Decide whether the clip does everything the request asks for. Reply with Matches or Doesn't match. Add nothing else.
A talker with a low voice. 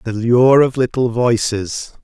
Matches